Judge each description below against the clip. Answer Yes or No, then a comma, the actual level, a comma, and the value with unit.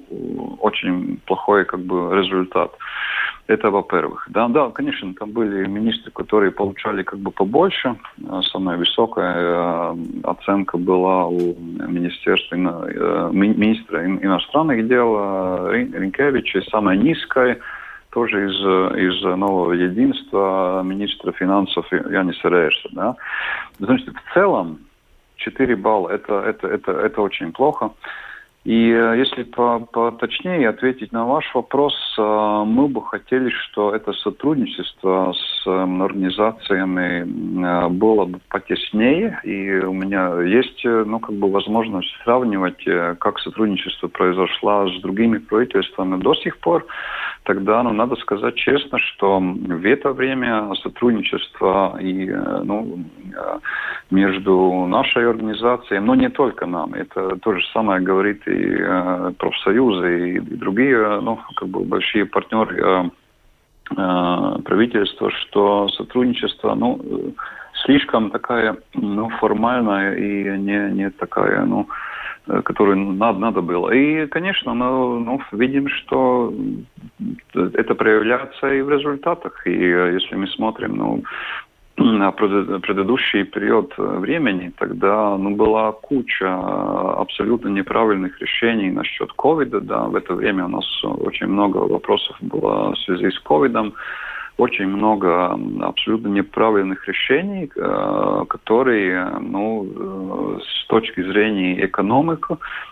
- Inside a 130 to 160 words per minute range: No, average, 115 wpm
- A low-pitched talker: Yes, low, 100 Hz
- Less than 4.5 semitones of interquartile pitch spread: Yes, average, 3.6 semitones